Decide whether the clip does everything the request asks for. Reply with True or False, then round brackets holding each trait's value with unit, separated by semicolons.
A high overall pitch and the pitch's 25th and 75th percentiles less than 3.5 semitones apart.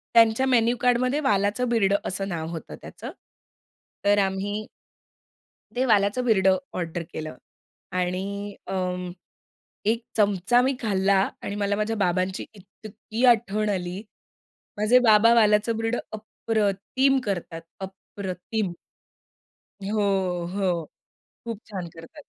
True (205 Hz; 3.1 semitones)